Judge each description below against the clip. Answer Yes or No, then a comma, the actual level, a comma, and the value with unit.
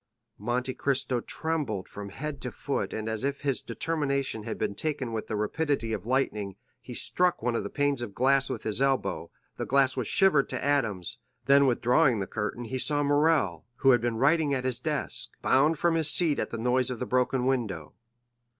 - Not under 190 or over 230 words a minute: Yes, average, 200 wpm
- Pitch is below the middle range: Yes, low, 130 Hz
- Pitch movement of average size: Yes, average, 3.8 semitones